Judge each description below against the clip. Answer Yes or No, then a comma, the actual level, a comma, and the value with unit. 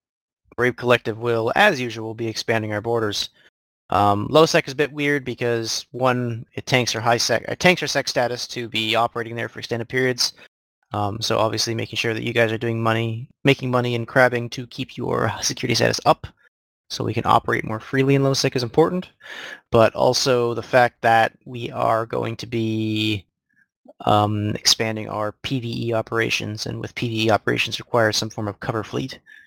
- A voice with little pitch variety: Yes, narrow, 2.3 semitones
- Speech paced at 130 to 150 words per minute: No, average, 185 wpm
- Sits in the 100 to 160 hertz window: Yes, low, 115 Hz